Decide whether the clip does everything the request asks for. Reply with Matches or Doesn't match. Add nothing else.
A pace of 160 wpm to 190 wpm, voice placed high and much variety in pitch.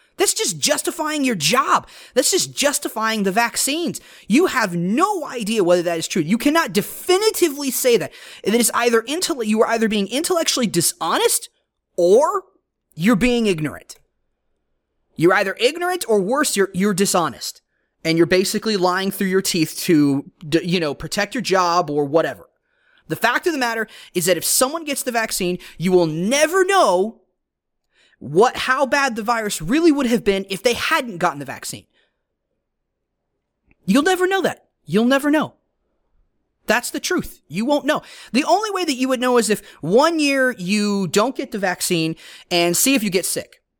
Matches